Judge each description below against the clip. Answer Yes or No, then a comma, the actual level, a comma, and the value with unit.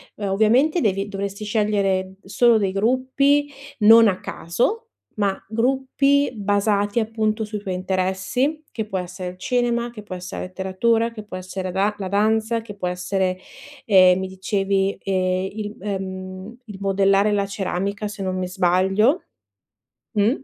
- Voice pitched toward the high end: Yes, high, 200 Hz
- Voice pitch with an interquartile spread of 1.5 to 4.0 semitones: Yes, average, 2.9 semitones